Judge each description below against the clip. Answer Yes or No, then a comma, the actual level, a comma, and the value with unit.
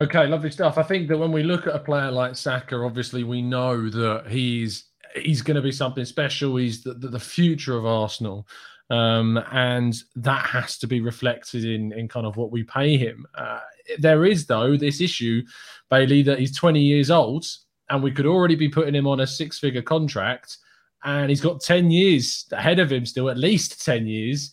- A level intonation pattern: No, average, 4.3 semitones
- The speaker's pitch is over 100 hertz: Yes, low, 135 Hz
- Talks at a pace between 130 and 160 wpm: No, average, 200 wpm